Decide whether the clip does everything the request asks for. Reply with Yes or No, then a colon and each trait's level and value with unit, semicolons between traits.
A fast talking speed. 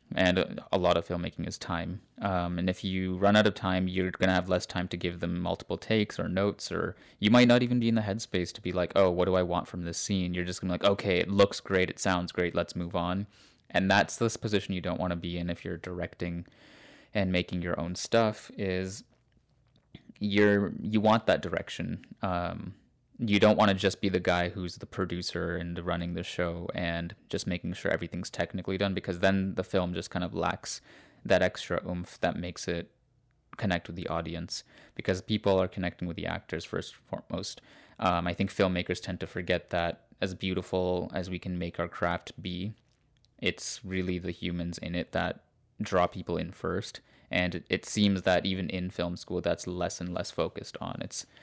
Yes: fast, 210 wpm